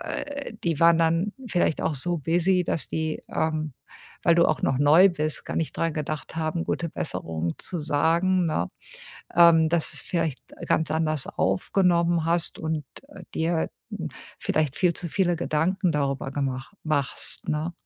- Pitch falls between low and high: Yes, medium, 160 Hz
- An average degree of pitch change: No, narrow, 2.3 semitones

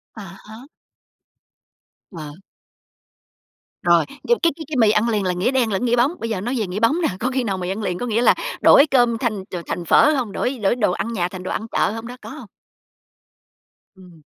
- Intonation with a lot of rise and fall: No, average, 4.6 semitones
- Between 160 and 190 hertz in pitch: No, high, 220 Hz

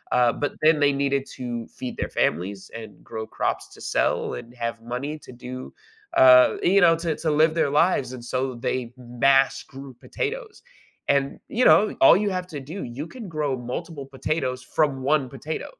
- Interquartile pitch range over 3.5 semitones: Yes, average, 3.9 semitones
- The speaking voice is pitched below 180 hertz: Yes, low, 135 Hz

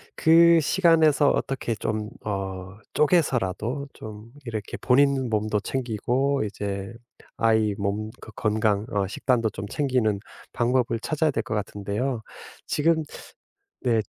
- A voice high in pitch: No, low, 115 Hz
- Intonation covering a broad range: No, average, 4.7 semitones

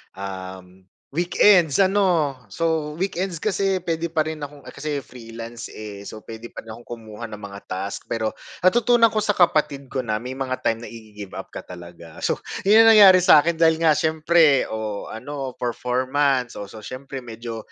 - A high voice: No, low, 130 Hz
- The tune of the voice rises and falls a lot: Yes, wide, 7.0 semitones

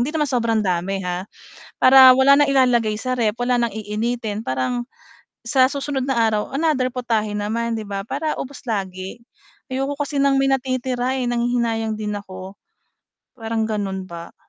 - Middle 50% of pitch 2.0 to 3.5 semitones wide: No, average, 3.9 semitones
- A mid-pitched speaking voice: No, high, 235 Hz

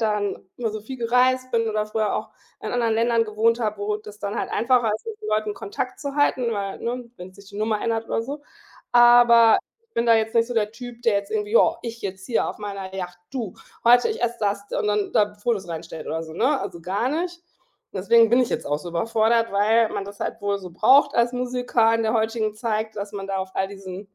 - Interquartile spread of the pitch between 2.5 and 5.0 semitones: Yes, average, 2.9 semitones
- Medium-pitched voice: No, high, 220 Hz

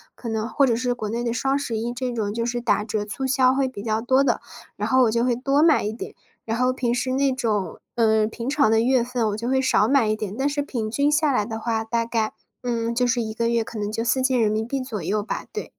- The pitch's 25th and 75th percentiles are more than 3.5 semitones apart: No, average, 2.8 semitones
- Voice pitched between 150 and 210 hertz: No, high, 235 Hz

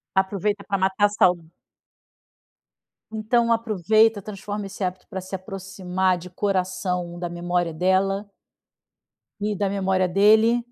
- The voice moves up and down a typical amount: No, narrow, 2.2 semitones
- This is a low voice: No, high, 190 Hz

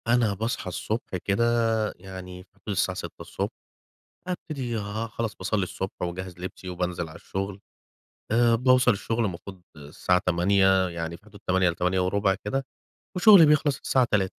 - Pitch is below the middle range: Yes, very low, 95 Hz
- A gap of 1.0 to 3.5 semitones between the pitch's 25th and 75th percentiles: No, average, 3.9 semitones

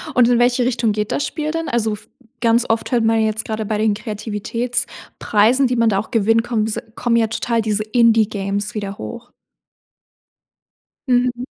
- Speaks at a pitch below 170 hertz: No, high, 225 Hz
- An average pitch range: No, narrow, 2.2 semitones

